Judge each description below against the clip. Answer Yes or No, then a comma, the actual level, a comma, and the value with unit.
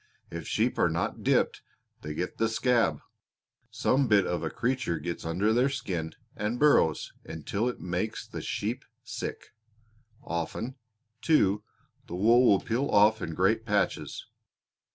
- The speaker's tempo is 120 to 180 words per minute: Yes, average, 145 wpm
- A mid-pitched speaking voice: No, low, 105 Hz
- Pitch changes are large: Yes, wide, 6.0 semitones